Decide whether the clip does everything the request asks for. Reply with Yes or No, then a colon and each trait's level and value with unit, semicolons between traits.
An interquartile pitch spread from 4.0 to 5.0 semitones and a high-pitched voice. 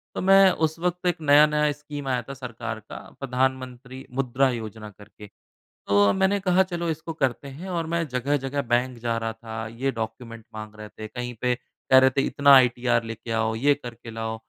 No: average, 4.5 semitones; low, 130 Hz